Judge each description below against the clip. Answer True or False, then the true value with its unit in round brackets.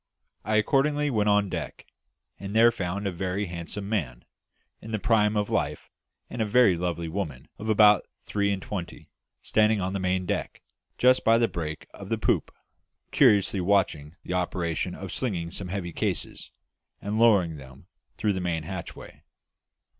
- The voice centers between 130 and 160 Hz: False (100 Hz)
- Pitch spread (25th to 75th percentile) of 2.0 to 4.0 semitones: True (3.5 semitones)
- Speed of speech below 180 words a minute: True (165 wpm)